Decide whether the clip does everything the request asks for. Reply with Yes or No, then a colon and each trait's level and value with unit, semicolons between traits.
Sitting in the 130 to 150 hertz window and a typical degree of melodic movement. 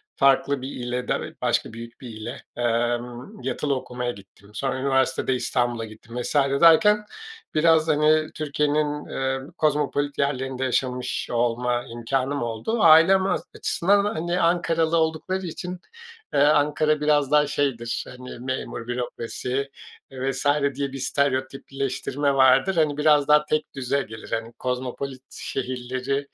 Yes: low, 135 Hz; average, 3.4 semitones